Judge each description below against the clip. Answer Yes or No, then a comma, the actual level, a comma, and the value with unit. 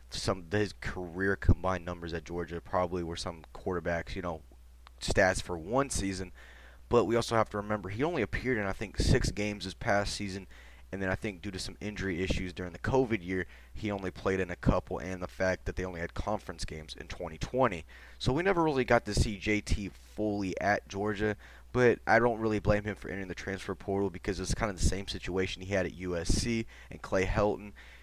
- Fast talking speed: Yes, fast, 215 wpm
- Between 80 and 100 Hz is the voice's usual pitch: Yes, very low, 95 Hz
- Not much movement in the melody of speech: No, average, 3.0 semitones